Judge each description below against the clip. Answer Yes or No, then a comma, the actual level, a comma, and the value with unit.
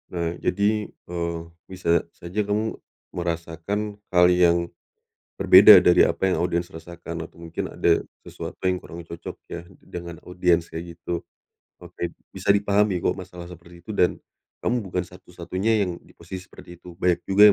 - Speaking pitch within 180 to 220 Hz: No, very low, 90 Hz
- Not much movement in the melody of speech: Yes, narrow, 2.1 semitones